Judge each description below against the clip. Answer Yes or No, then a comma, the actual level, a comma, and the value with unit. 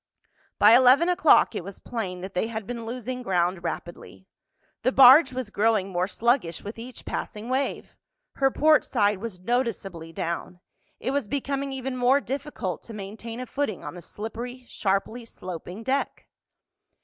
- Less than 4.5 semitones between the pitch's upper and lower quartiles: No, average, 5.0 semitones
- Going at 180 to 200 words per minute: No, average, 150 wpm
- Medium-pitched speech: No, high, 230 Hz